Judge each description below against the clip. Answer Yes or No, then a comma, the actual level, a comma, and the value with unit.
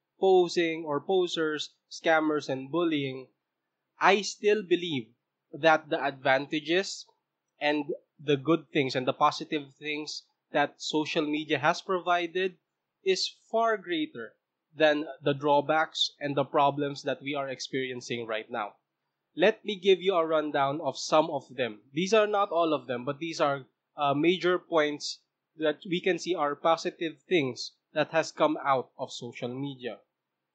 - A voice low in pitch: No, medium, 155 Hz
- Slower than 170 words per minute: Yes, average, 150 wpm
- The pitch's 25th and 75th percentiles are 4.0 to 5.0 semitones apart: No, average, 3.6 semitones